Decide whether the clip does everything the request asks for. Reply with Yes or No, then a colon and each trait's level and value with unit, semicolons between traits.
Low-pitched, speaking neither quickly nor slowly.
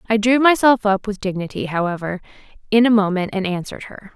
No: high, 210 Hz; average, 190 wpm